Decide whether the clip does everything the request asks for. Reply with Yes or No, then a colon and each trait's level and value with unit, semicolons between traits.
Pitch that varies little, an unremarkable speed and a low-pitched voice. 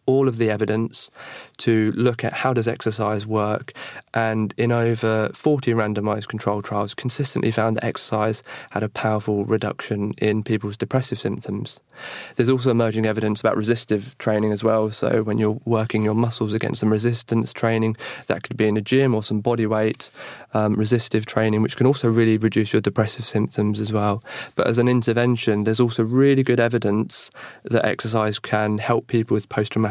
Yes: narrow, 1.6 semitones; average, 180 wpm; low, 110 Hz